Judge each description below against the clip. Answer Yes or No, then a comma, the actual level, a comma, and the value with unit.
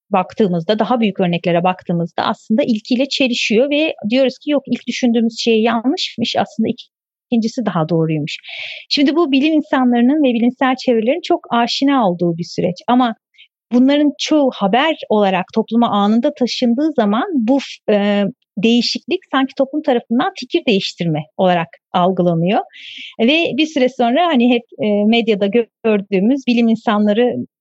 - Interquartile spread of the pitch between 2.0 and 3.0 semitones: No, average, 4.4 semitones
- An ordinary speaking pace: Yes, average, 130 wpm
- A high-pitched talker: Yes, high, 240 Hz